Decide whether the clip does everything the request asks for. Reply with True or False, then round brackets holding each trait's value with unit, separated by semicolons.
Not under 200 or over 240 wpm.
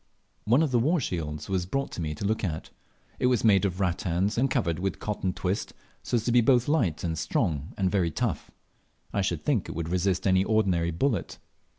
True (205 wpm)